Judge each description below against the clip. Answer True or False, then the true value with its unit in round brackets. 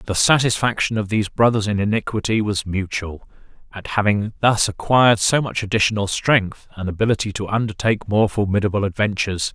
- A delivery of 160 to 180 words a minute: False (150 wpm)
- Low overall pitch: True (105 Hz)